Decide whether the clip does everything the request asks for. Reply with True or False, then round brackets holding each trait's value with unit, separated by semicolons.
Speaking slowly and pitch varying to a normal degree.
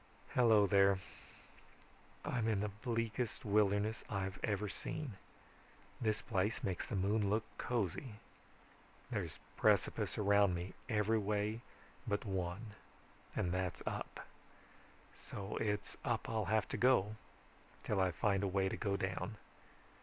False (130 wpm; 2.1 semitones)